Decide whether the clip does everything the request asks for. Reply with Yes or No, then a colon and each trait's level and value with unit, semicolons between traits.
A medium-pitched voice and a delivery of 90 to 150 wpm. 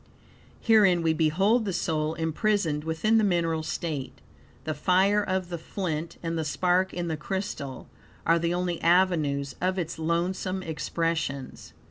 Yes: medium, 170 Hz; average, 145 wpm